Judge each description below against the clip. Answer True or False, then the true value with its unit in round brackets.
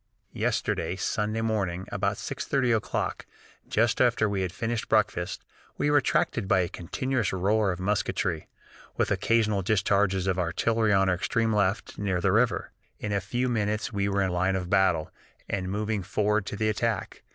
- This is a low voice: True (100 Hz)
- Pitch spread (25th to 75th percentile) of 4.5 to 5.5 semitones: False (2.8 semitones)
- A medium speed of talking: True (170 wpm)